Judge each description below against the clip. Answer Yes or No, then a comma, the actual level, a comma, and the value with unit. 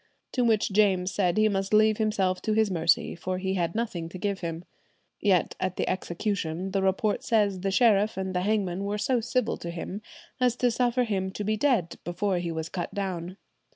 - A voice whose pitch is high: Yes, high, 195 Hz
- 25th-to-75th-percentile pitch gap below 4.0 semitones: Yes, average, 3.0 semitones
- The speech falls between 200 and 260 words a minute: Yes, fast, 205 wpm